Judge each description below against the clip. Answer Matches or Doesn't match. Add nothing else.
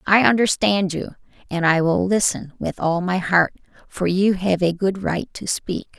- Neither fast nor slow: Matches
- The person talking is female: Matches